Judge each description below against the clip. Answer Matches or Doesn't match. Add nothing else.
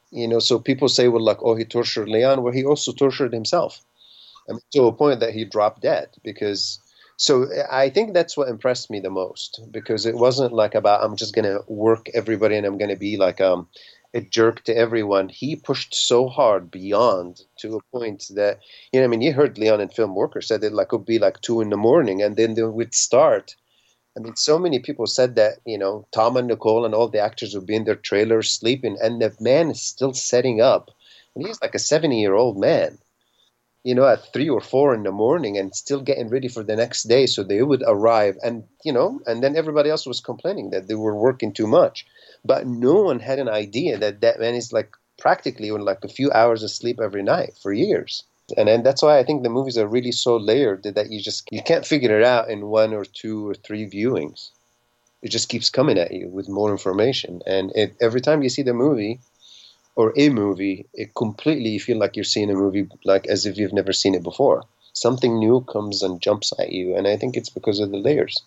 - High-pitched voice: Doesn't match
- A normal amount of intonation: Matches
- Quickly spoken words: Matches